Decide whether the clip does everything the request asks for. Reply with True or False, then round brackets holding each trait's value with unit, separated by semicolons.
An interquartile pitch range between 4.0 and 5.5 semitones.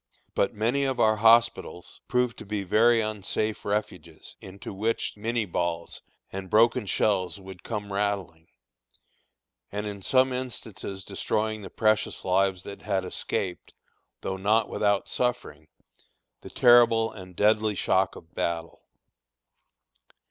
False (2.9 semitones)